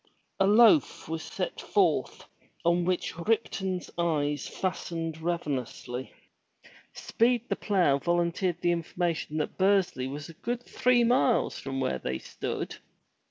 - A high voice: No, medium, 175 Hz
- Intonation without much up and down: No, average, 4.6 semitones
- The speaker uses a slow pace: Yes, slow, 125 wpm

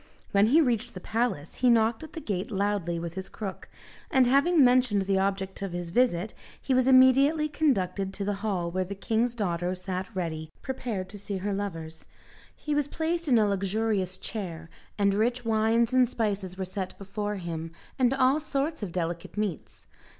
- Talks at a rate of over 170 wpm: Yes, average, 185 wpm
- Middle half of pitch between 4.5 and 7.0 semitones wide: Yes, average, 4.9 semitones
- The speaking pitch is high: Yes, high, 205 Hz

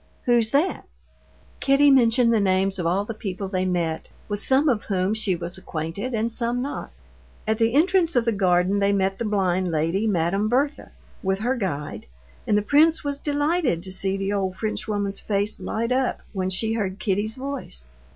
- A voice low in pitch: No, high, 205 Hz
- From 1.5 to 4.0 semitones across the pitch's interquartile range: No, average, 4.4 semitones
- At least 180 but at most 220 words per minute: Yes, average, 185 wpm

